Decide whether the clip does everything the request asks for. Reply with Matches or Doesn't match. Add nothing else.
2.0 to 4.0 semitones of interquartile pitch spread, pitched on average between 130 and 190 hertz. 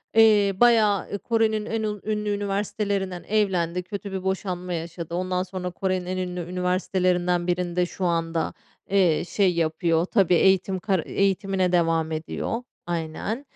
Matches